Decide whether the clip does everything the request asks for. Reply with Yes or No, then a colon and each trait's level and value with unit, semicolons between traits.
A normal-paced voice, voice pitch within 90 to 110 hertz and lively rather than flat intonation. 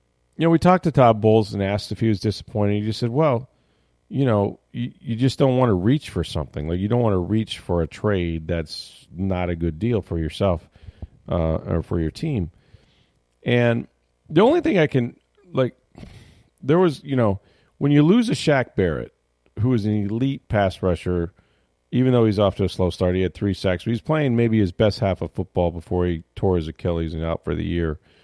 No: fast, 220 wpm; low, 100 Hz; wide, 5.9 semitones